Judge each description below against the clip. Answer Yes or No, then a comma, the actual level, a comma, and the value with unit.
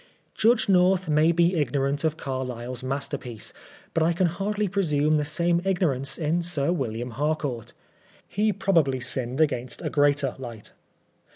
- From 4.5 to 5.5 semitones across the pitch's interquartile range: Yes, average, 4.8 semitones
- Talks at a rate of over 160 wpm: No, average, 145 wpm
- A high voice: No, medium, 150 Hz